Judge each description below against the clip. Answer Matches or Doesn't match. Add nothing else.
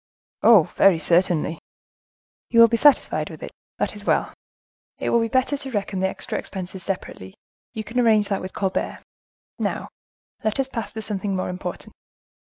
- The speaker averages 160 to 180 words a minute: Matches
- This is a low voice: Doesn't match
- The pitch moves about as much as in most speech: Matches